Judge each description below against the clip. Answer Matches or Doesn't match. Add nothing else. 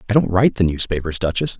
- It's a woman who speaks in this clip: Doesn't match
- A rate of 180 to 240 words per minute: Matches